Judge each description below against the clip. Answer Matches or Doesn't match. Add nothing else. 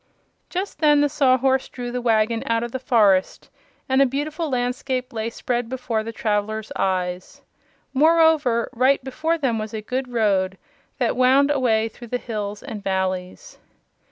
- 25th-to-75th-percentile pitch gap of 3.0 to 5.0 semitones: Matches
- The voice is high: Matches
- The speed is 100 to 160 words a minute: Matches